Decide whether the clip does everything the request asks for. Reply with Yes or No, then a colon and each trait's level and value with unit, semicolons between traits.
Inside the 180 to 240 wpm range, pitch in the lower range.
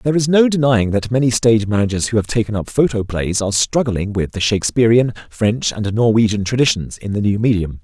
Yes: average, 200 wpm; low, 110 Hz